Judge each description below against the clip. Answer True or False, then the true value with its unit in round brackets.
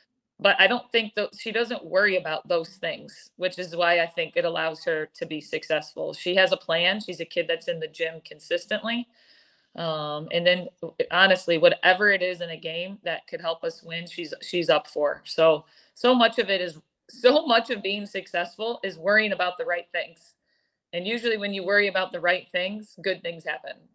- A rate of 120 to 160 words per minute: False (205 wpm)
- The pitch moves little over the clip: False (5.0 semitones)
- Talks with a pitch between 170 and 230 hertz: True (185 Hz)